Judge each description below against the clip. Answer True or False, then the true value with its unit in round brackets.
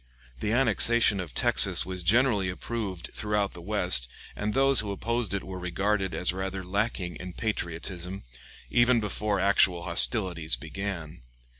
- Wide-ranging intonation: False (3.0 semitones)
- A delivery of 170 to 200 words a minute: False (140 wpm)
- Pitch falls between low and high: False (100 Hz)